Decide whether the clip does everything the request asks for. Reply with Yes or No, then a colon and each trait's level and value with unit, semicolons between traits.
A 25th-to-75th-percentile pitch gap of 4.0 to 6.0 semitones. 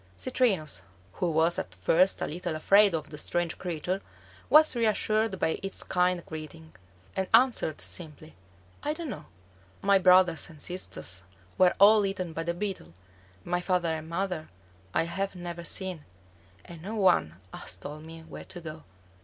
No: average, 3.4 semitones